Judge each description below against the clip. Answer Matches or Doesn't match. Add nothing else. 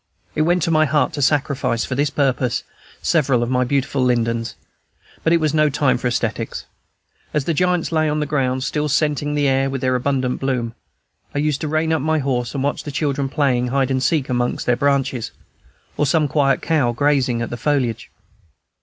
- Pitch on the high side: Doesn't match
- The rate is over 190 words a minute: Matches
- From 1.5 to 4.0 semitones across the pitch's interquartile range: Matches